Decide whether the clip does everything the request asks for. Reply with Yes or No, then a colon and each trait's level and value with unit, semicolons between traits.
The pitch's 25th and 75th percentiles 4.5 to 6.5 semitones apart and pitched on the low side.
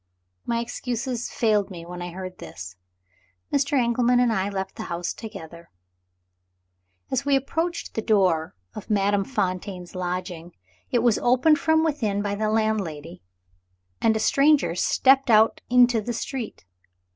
No: average, 5.3 semitones; high, 215 Hz